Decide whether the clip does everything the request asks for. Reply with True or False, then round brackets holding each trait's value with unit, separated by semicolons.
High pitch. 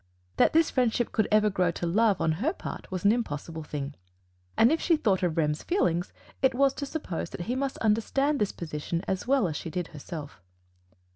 True (200 Hz)